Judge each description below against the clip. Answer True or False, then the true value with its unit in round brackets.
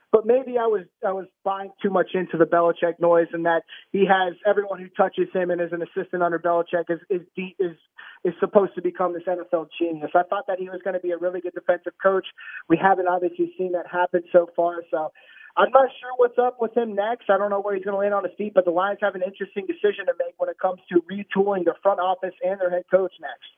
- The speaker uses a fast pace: True (250 wpm)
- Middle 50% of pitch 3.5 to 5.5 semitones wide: False (2.4 semitones)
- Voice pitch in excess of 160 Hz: True (185 Hz)